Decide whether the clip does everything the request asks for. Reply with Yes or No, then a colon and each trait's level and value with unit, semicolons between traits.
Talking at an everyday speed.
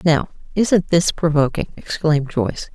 No: slow, 130 wpm